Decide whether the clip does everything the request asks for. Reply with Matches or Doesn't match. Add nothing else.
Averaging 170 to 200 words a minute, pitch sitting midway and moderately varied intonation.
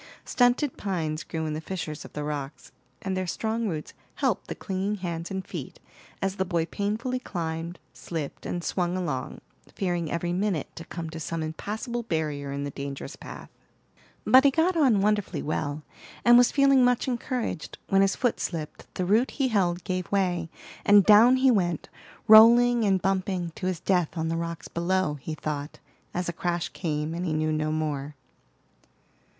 Matches